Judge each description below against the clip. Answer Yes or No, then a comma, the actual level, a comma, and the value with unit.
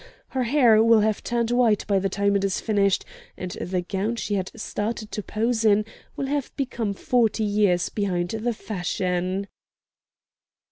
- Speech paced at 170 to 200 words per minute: No, average, 155 wpm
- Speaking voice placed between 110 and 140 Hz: No, high, 210 Hz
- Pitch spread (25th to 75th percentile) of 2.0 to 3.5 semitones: Yes, average, 2.8 semitones